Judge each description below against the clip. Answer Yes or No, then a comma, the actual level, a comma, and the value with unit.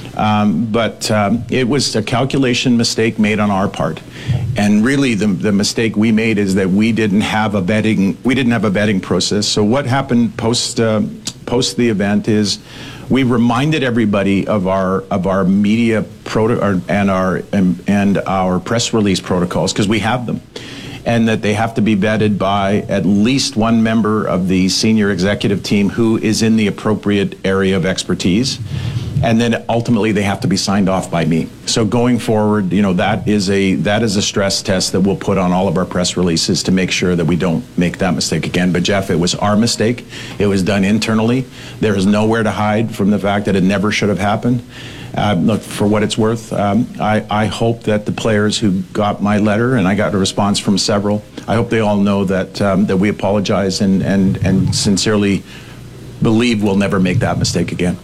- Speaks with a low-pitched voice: Yes, low, 105 Hz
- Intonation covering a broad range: No, average, 2.7 semitones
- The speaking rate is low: No, fast, 205 wpm